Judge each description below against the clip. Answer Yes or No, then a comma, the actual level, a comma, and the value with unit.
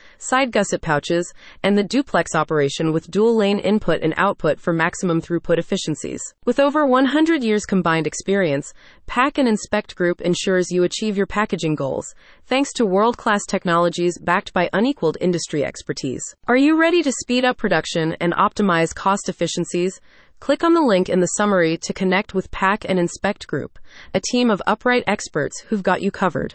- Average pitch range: Yes, average, 4.1 semitones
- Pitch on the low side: No, high, 195 Hz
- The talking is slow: No, average, 175 wpm